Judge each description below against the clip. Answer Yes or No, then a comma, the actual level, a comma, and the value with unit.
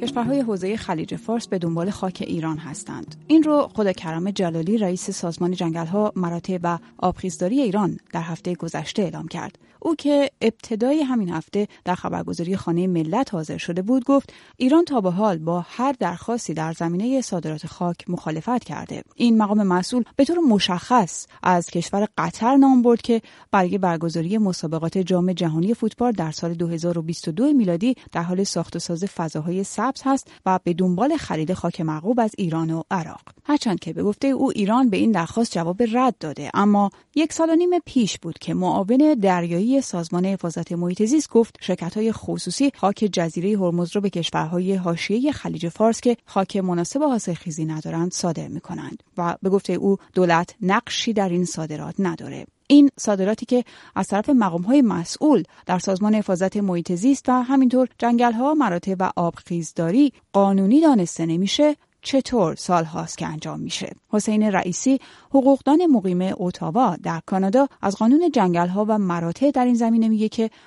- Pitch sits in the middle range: No, high, 195 Hz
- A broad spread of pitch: Yes, wide, 5.7 semitones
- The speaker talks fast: Yes, fast, 165 wpm